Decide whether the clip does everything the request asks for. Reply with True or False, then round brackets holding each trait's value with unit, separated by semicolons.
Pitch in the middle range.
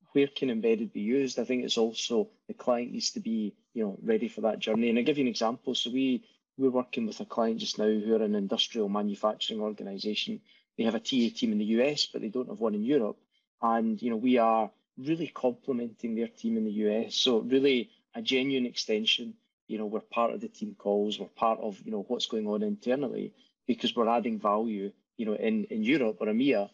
False (125 Hz)